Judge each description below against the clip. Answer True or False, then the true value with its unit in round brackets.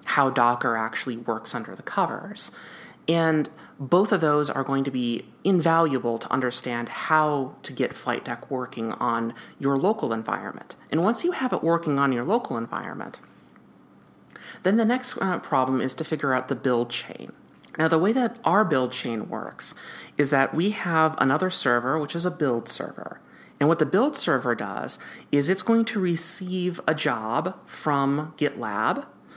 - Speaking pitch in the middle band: True (150 Hz)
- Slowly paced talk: False (170 wpm)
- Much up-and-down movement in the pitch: True (5.8 semitones)